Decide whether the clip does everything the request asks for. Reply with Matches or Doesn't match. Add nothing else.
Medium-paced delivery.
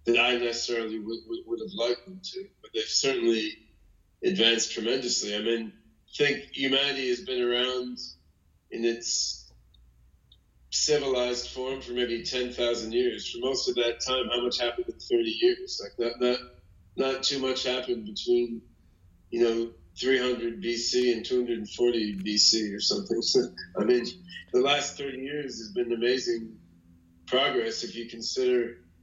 Matches